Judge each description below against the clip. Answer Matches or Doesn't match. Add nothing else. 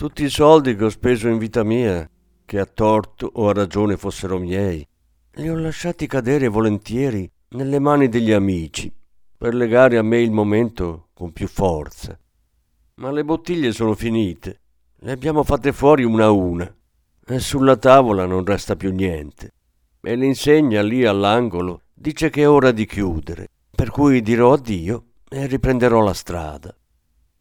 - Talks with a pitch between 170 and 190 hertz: Doesn't match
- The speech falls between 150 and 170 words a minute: Matches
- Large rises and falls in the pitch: Matches